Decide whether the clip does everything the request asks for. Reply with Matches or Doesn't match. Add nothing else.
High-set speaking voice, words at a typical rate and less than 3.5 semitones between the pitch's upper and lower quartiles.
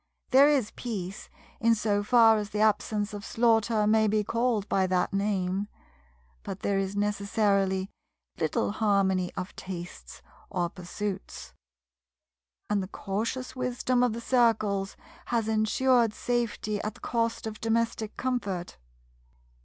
Doesn't match